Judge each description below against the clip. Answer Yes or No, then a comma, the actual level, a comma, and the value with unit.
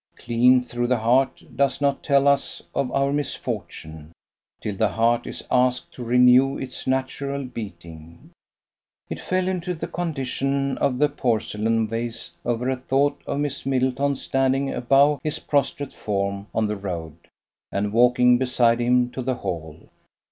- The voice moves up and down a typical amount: Yes, average, 3.4 semitones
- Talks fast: No, average, 150 wpm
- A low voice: Yes, low, 125 Hz